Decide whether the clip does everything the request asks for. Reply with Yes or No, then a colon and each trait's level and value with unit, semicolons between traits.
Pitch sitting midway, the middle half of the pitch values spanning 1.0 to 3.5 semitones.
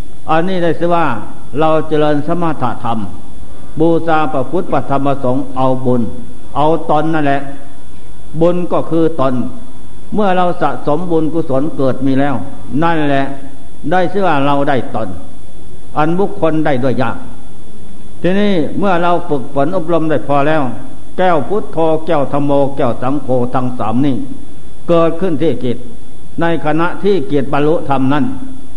No: medium, 145 Hz; average, 4.1 semitones